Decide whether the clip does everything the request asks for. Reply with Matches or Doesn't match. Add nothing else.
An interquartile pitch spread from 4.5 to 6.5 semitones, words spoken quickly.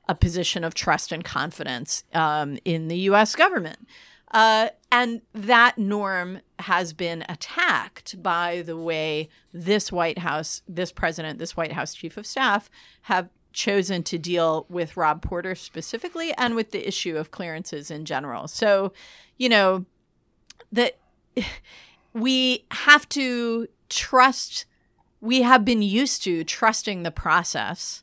Doesn't match